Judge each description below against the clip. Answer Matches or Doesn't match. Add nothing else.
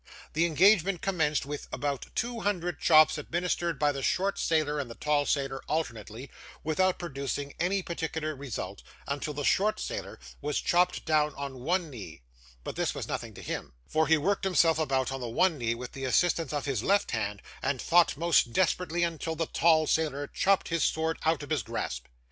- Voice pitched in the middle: Matches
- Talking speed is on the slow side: Doesn't match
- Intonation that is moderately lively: Matches